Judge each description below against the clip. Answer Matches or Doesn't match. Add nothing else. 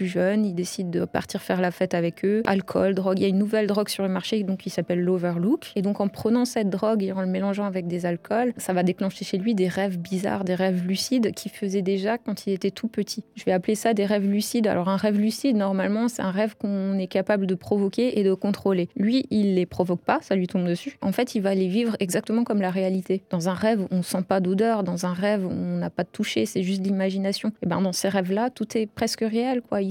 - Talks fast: Matches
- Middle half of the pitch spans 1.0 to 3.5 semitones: Matches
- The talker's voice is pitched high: Matches